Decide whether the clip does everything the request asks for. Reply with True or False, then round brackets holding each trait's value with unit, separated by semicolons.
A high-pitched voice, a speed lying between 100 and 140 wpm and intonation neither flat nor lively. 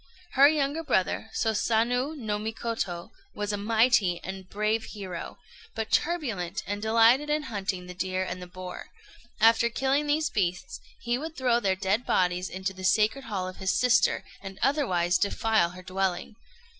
False (210 Hz; 165 wpm; 4.6 semitones)